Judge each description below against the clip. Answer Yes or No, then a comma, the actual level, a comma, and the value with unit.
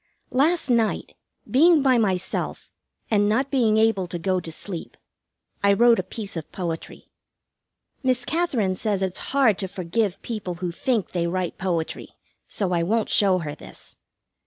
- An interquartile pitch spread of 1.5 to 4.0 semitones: No, average, 4.7 semitones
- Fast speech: No, average, 160 wpm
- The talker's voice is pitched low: No, high, 200 Hz